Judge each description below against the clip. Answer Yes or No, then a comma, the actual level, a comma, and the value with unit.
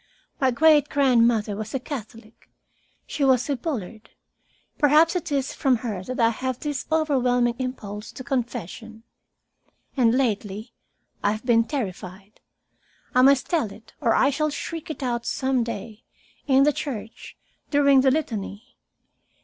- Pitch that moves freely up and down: No, average, 4.0 semitones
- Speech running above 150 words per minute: No, average, 145 wpm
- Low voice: No, very high, 250 Hz